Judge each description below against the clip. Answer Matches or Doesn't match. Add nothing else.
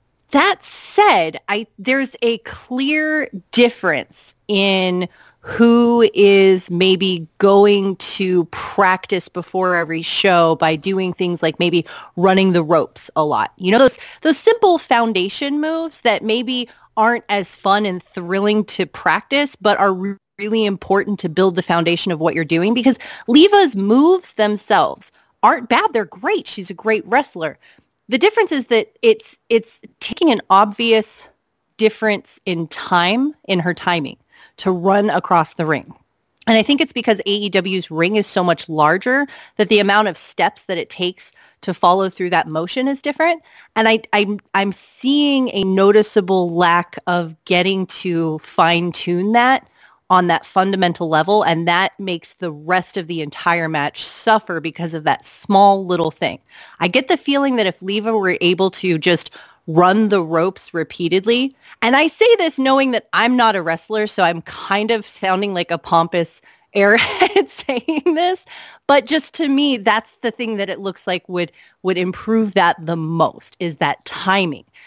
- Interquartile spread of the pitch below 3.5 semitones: Doesn't match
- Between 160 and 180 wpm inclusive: Matches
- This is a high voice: Matches